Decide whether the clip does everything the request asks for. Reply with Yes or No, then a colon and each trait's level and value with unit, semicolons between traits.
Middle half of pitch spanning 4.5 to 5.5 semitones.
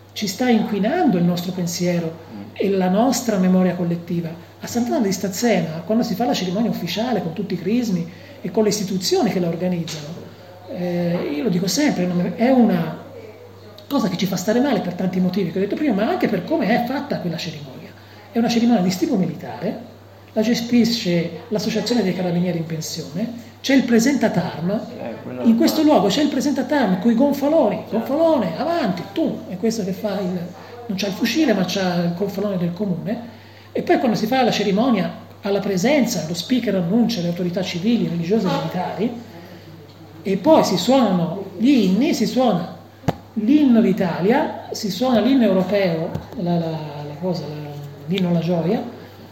Yes: average, 4.8 semitones